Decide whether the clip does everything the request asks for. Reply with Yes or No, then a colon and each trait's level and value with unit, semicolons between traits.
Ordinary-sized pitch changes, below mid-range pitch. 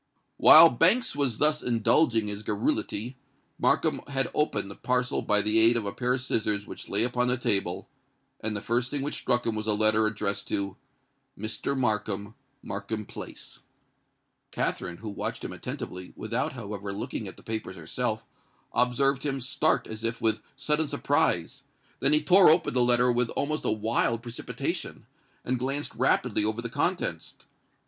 Yes: average, 3.5 semitones; low, 115 Hz